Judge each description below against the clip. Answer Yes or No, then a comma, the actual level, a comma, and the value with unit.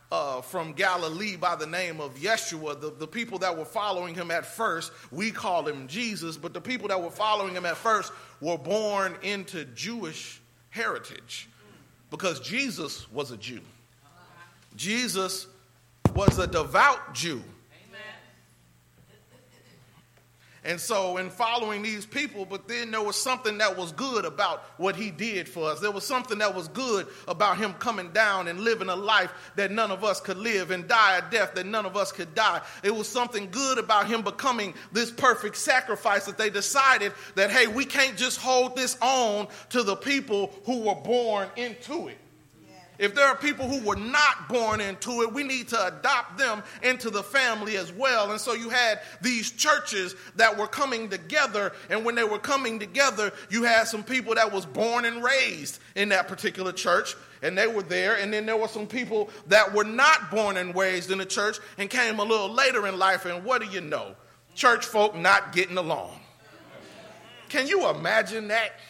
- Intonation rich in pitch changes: No, average, 4.1 semitones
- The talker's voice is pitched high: Yes, high, 210 Hz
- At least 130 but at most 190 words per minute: Yes, average, 185 wpm